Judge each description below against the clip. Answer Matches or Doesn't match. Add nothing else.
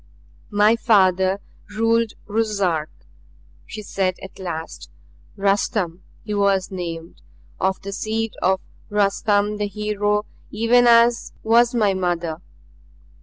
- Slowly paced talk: Matches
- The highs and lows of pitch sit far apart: Doesn't match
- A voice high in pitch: Matches